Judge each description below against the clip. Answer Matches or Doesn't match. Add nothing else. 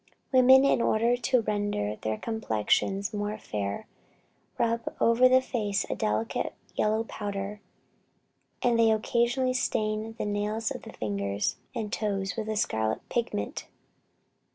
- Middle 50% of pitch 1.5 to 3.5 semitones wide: Matches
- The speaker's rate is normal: Doesn't match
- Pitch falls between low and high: Doesn't match